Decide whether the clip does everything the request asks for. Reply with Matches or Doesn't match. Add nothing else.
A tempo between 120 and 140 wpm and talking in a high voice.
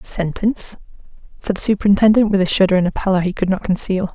Doesn't match